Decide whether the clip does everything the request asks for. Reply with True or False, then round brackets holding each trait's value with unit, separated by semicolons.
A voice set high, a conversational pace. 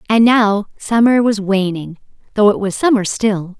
True (210 Hz; 165 wpm)